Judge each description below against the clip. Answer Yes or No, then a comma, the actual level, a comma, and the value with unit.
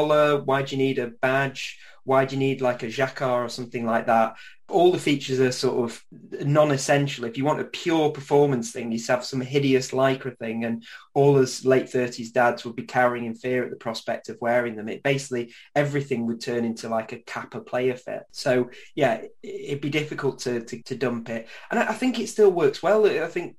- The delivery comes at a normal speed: No, fast, 215 wpm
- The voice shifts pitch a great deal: No, average, 2.8 semitones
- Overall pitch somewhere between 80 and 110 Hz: No, low, 130 Hz